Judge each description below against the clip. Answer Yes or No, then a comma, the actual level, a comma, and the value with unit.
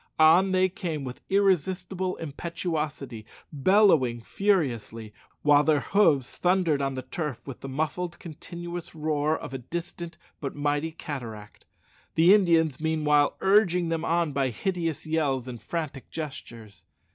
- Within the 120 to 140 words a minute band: Yes, slow, 135 wpm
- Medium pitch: Yes, medium, 155 Hz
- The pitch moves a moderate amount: Yes, average, 4.1 semitones